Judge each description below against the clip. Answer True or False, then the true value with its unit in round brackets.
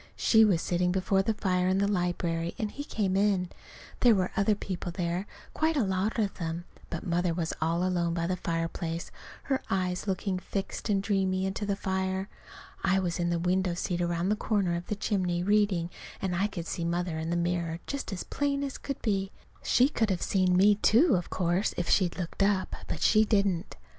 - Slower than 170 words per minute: False (205 wpm)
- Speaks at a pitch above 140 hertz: True (185 Hz)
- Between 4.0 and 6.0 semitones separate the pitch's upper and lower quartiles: False (2.7 semitones)